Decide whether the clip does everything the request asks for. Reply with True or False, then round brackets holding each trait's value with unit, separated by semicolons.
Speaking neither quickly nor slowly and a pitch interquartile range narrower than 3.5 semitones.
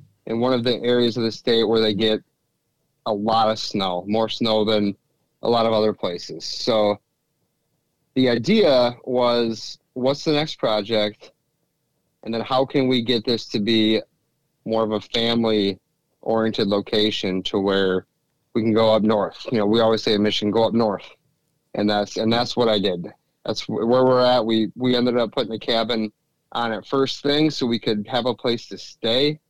True (185 wpm; 2.7 semitones)